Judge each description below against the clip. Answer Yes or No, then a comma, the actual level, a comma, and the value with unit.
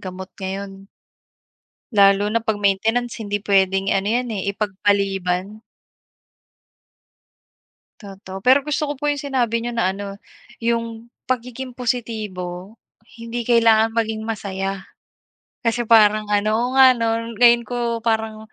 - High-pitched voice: Yes, high, 220 Hz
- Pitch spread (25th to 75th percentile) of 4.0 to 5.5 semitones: No, average, 3.1 semitones